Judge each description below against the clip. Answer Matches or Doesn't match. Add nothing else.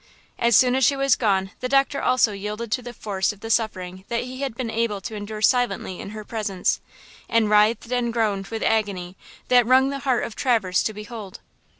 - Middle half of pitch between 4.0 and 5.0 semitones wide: Doesn't match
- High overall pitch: Matches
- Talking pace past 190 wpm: Matches